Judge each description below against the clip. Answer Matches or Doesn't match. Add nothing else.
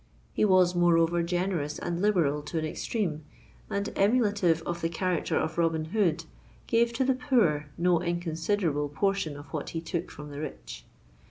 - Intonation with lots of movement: Doesn't match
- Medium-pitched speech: Matches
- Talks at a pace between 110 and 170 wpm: Matches